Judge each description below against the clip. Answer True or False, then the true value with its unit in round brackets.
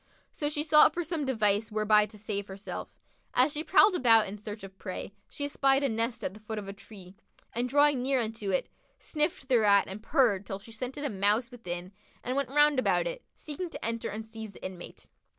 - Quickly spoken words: True (215 wpm)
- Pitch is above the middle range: True (230 Hz)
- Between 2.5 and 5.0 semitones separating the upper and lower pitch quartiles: False (5.4 semitones)